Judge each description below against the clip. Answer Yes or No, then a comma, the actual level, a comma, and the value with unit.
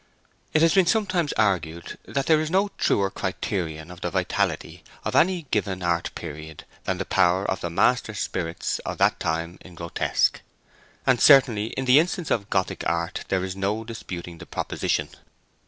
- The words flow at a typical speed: Yes, average, 170 wpm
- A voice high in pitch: No, very low, 95 Hz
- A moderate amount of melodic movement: No, wide, 7.8 semitones